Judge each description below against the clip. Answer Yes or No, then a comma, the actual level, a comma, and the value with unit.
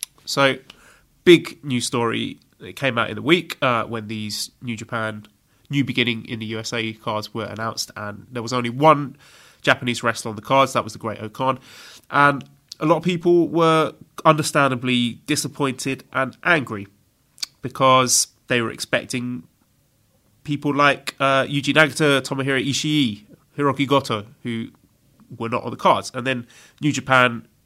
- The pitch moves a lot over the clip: No, average, 3.6 semitones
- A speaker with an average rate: Yes, average, 155 wpm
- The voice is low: Yes, low, 130 Hz